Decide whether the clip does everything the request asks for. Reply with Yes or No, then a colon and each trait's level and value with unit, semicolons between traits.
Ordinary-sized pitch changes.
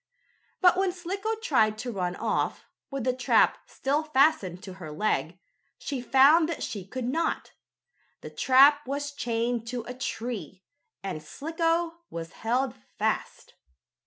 No: wide, 6.3 semitones